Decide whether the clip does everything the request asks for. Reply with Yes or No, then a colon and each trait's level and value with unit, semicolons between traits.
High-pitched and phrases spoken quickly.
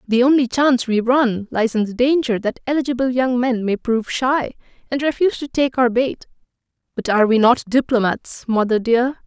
No: high, 245 Hz; average, 190 wpm